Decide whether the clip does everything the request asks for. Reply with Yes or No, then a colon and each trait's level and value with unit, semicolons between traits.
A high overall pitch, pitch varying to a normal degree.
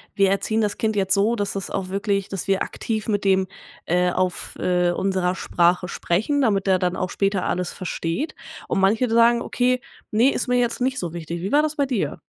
Yes: high, 195 Hz; average, 3.8 semitones